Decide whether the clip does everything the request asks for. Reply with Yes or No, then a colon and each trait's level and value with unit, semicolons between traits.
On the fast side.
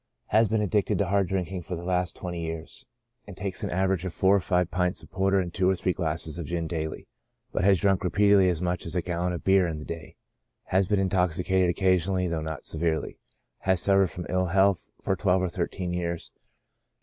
Yes: fast, 220 wpm